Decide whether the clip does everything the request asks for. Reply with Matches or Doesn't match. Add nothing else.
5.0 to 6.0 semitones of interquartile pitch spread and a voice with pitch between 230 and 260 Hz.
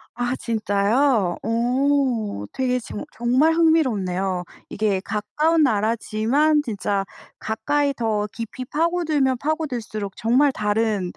Matches